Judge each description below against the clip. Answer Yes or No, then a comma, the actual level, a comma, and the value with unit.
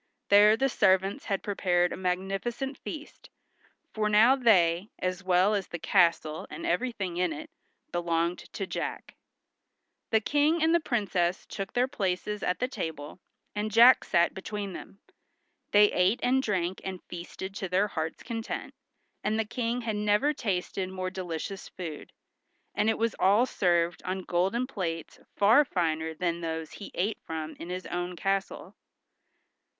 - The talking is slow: No, average, 155 wpm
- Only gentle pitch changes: No, average, 3.8 semitones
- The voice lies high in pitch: Yes, high, 195 Hz